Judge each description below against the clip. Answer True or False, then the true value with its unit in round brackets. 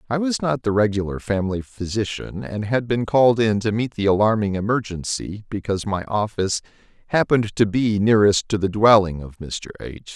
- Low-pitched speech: True (105 Hz)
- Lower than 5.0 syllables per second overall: False (5.5 syllables/s)